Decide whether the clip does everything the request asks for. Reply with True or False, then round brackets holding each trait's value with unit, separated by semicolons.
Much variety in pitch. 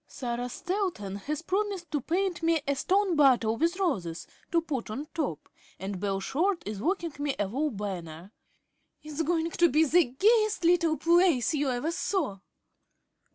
True (6.7 semitones)